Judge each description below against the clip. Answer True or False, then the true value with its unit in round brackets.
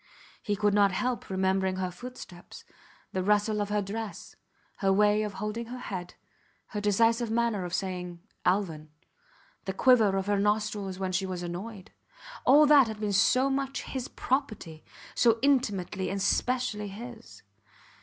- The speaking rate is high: False (155 wpm)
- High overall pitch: True (205 Hz)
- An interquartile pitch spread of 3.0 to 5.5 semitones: True (3.5 semitones)